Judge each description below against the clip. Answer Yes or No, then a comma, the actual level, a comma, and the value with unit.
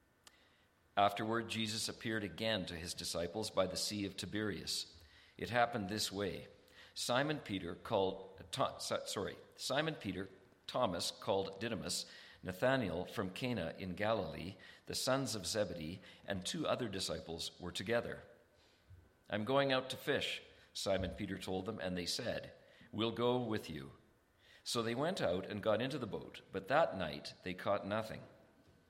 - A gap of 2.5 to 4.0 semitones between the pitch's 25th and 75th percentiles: Yes, average, 3.6 semitones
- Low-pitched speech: Yes, low, 100 Hz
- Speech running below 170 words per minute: Yes, average, 150 wpm